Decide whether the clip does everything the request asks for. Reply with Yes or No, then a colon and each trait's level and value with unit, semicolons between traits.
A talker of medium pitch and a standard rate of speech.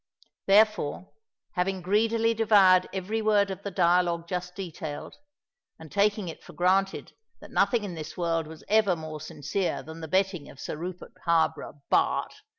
Yes: medium, 180 Hz; average, 155 wpm